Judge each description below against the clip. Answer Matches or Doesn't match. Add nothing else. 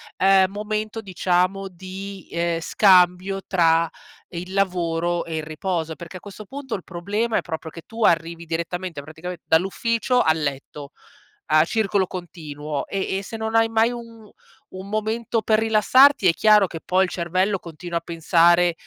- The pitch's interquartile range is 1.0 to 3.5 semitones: Doesn't match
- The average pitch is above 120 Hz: Matches